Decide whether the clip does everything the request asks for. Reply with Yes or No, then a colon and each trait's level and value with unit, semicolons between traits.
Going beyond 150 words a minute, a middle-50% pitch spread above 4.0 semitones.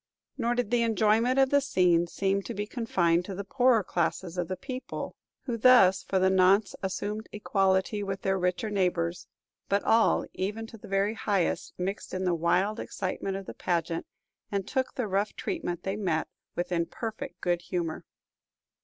No: average, 180 wpm; average, 3.5 semitones